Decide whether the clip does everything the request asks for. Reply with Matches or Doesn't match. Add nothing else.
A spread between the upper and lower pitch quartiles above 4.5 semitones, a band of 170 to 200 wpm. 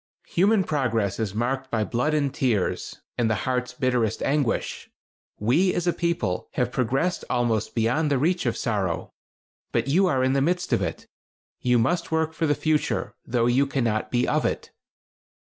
Matches